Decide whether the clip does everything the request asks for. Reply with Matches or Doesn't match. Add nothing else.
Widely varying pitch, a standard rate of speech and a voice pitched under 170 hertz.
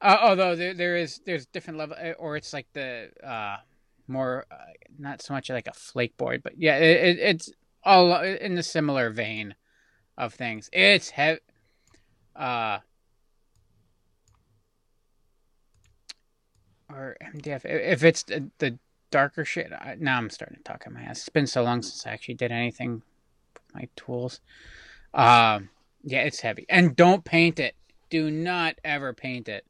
Matches